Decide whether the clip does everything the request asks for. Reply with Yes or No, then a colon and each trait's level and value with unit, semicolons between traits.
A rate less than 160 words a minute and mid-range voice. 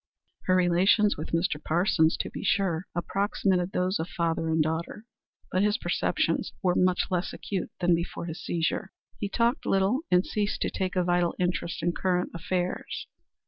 No: average, 170 wpm; medium, 180 Hz